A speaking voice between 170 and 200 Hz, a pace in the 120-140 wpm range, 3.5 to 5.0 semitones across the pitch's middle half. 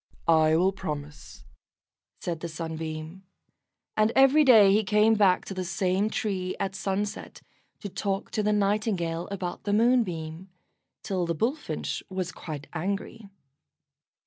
Yes: high, 190 Hz; slow, 135 wpm; average, 3.8 semitones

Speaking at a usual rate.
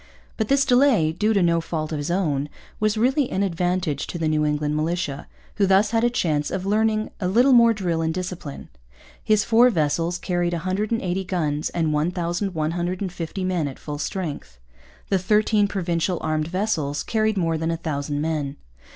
Yes: average, 170 wpm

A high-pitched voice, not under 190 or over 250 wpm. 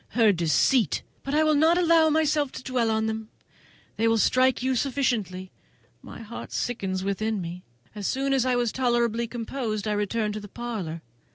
No: high, 230 Hz; average, 180 wpm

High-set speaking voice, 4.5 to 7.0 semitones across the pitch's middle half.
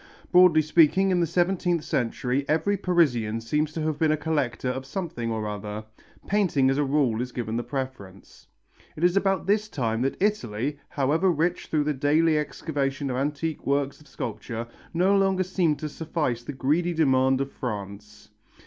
No: medium, 145 Hz; average, 5.1 semitones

